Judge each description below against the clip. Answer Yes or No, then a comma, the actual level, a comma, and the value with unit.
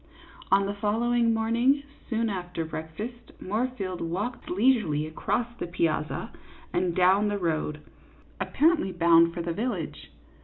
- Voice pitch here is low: No, high, 195 Hz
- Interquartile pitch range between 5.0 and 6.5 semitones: Yes, wide, 5.5 semitones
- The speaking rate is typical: No, slow, 125 wpm